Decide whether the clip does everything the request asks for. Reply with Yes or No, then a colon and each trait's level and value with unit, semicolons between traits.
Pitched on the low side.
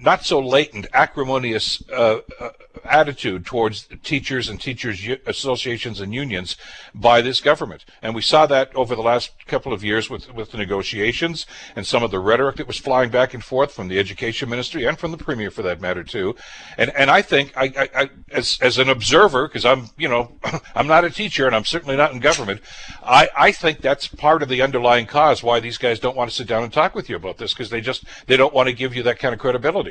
Yes: low, 125 Hz